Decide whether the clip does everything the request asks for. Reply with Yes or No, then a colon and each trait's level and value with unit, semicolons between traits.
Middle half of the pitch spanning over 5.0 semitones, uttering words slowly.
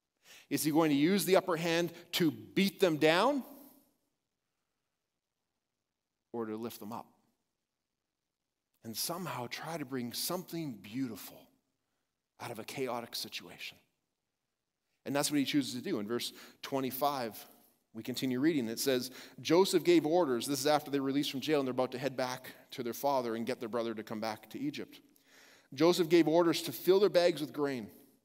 No: wide, 5.6 semitones; average, 170 wpm